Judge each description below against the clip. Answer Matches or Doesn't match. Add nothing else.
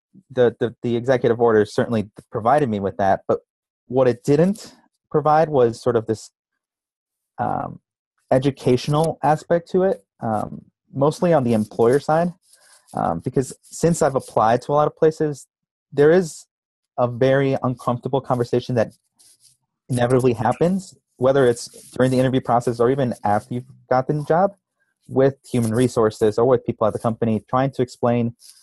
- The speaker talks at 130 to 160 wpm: Matches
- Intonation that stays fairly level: Doesn't match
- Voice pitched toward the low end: Matches